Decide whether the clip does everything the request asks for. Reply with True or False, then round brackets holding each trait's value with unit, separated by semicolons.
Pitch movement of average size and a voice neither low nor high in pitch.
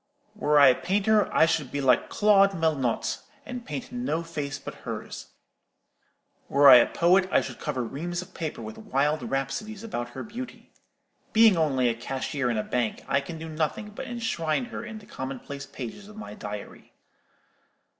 False (7.4 semitones; 155 Hz)